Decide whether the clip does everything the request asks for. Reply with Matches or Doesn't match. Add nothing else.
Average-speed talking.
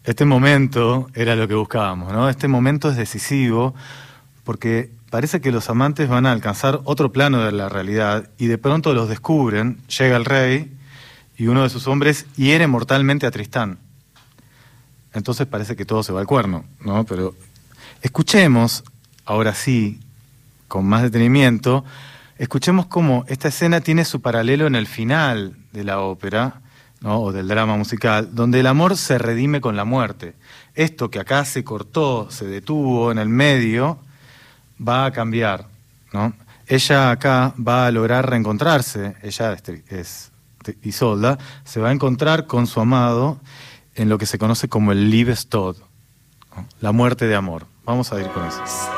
Matches